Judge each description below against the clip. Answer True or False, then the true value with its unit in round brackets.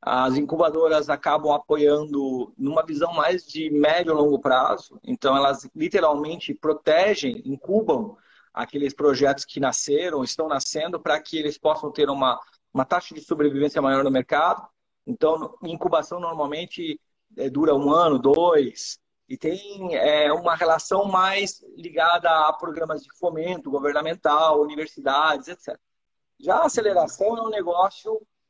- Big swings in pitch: False (3.7 semitones)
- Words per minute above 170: False (135 wpm)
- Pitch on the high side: False (155 Hz)